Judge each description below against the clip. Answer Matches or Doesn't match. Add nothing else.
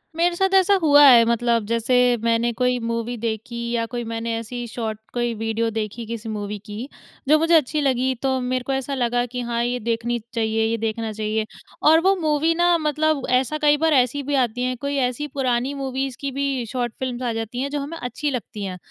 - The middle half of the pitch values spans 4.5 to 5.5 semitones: Doesn't match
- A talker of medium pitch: Doesn't match